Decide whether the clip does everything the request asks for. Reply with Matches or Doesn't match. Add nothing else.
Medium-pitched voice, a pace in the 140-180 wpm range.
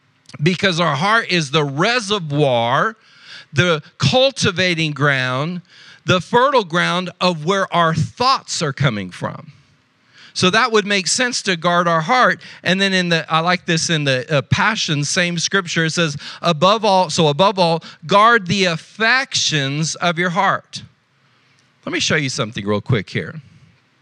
Matches